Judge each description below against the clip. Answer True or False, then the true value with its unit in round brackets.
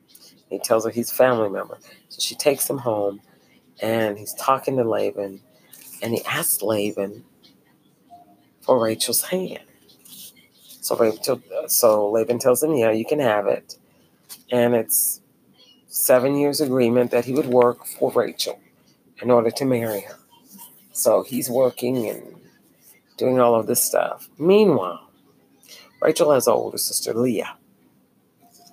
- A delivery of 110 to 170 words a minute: True (140 wpm)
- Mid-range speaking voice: False (120 Hz)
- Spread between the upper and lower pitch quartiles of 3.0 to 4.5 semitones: True (3.3 semitones)